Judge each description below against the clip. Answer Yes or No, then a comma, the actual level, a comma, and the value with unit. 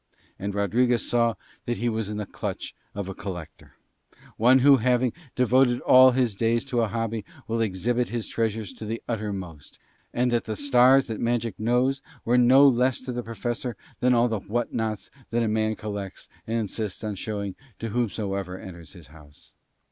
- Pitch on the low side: Yes, low, 115 Hz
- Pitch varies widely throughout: No, average, 3.0 semitones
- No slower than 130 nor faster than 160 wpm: No, average, 180 wpm